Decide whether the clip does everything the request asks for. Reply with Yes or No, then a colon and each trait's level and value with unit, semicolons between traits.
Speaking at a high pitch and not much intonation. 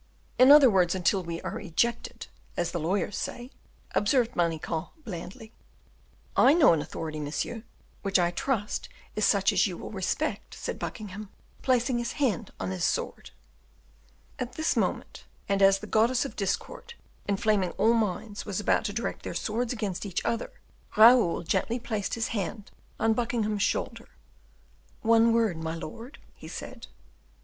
No: high, 210 Hz; average, 4.1 semitones